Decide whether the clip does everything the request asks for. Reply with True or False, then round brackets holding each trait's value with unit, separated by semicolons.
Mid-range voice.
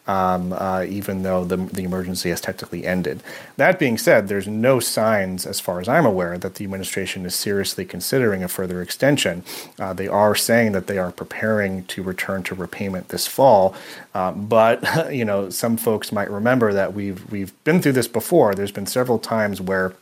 False (95 Hz)